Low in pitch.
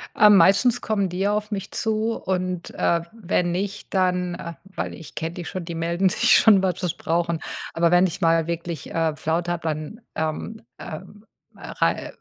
No: medium, 180 Hz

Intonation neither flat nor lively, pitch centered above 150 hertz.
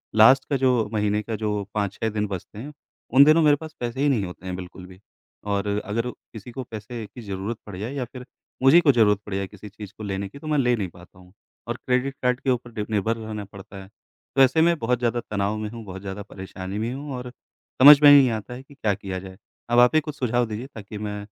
No: average, 3.9 semitones; low, 110 Hz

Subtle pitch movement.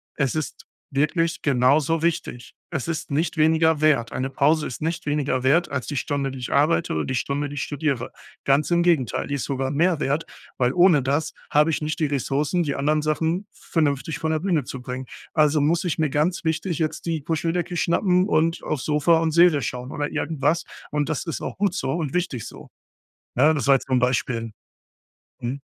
No: average, 3.1 semitones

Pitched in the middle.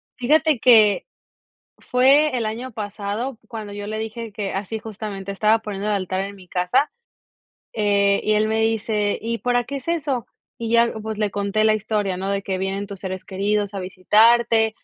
No: high, 215 Hz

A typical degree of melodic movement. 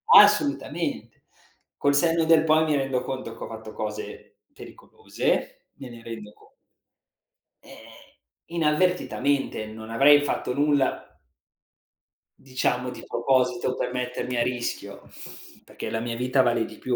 Yes: average, 3.8 semitones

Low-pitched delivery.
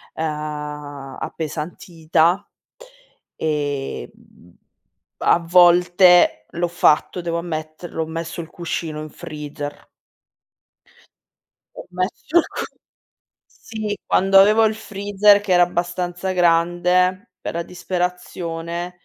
No: medium, 175 Hz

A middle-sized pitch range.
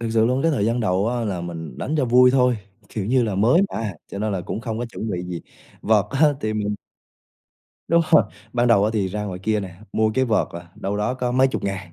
Yes: average, 4.0 semitones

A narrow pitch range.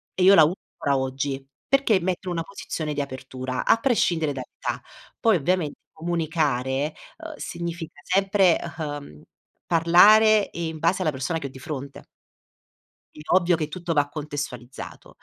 No: average, 4.4 semitones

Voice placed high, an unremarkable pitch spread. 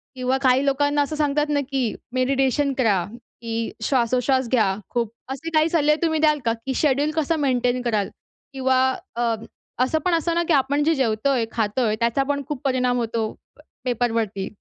Yes: very high, 260 Hz; average, 3.7 semitones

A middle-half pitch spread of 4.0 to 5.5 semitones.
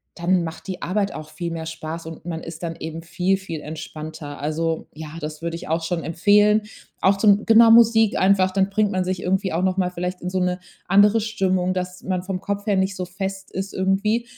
No: average, 3.1 semitones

